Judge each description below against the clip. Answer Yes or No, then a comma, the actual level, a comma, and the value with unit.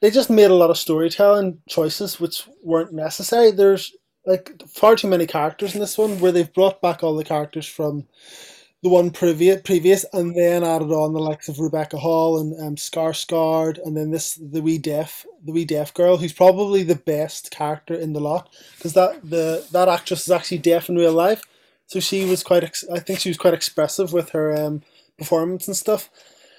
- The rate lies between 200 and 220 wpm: Yes, fast, 205 wpm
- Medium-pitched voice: Yes, medium, 170 Hz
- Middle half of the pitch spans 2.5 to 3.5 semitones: Yes, average, 2.8 semitones